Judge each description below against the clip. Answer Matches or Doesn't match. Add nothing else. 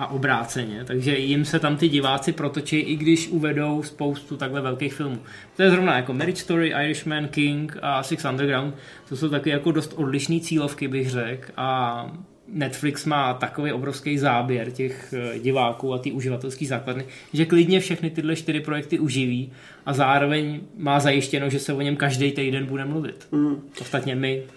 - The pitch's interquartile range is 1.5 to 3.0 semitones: Matches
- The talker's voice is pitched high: Doesn't match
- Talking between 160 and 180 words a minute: Matches